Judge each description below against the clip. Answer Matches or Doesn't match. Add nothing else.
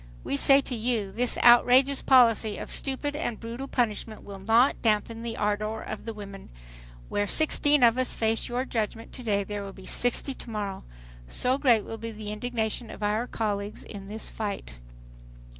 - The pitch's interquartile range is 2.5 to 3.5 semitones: Matches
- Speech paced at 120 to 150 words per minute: Doesn't match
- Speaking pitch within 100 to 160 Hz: Doesn't match